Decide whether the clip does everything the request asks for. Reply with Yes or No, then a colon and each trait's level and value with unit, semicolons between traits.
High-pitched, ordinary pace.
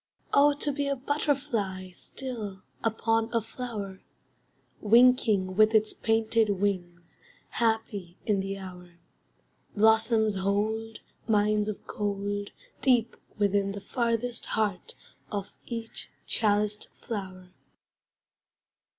No: high, 215 Hz; slow, 100 wpm